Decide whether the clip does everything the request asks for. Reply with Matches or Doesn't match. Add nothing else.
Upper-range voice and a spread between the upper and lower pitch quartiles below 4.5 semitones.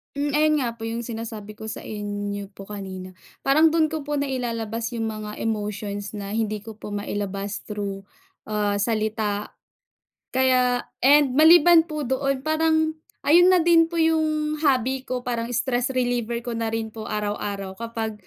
Doesn't match